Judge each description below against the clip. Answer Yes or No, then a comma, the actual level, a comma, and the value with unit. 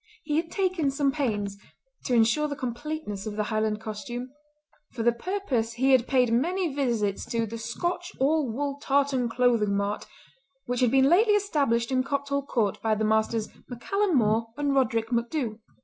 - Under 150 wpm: No, average, 170 wpm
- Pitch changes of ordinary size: Yes, average, 4.3 semitones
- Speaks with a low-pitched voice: No, very high, 250 Hz